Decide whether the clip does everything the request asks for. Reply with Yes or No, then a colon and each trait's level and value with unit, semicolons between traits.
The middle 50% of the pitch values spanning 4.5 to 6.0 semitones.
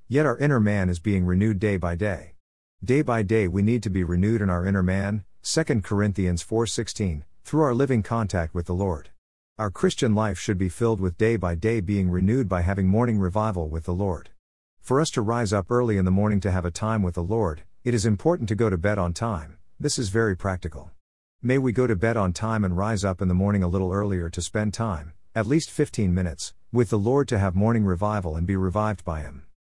No: average, 3.9 semitones